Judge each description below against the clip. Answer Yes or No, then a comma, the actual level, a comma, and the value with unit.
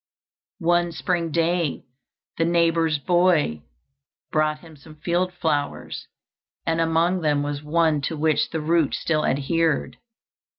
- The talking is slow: Yes, slow, 125 wpm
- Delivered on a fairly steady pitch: Yes, narrow, 1.9 semitones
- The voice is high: No, medium, 165 Hz